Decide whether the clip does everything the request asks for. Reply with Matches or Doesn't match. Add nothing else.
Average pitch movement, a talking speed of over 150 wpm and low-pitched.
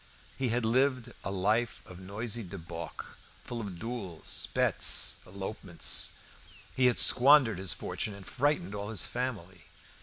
Doesn't match